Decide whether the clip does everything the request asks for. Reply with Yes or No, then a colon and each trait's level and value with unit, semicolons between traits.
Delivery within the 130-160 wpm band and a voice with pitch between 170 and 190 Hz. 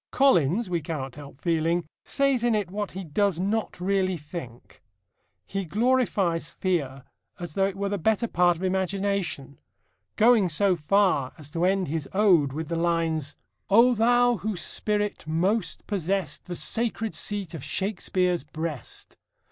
Yes: average, 150 wpm; medium, 185 Hz